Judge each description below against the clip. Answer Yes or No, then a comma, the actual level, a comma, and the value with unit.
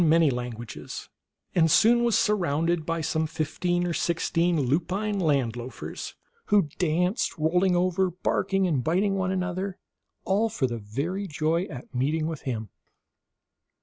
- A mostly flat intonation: No, average, 3.8 semitones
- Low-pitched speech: No, medium, 170 Hz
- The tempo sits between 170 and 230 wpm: No, average, 145 wpm